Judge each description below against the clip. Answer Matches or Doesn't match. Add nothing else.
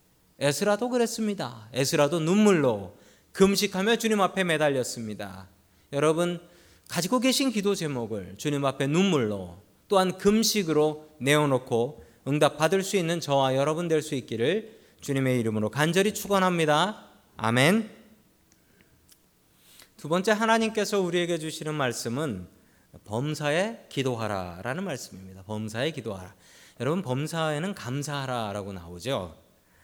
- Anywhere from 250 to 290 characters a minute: Doesn't match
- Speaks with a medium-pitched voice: Matches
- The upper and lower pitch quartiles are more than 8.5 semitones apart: Matches